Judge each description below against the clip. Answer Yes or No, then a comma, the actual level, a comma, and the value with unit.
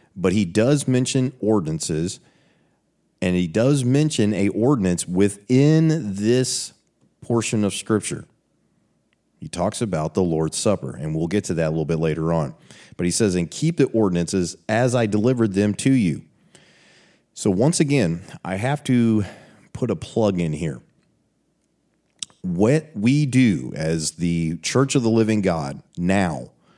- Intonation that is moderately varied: No, wide, 6.6 semitones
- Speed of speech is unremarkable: Yes, average, 150 wpm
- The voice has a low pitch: Yes, low, 105 Hz